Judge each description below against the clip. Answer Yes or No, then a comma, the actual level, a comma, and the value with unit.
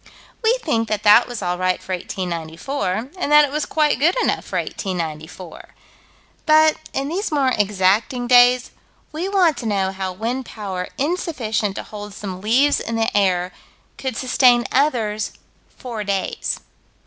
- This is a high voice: Yes, high, 225 Hz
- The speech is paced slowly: No, average, 155 wpm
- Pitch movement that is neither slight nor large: No, wide, 6.4 semitones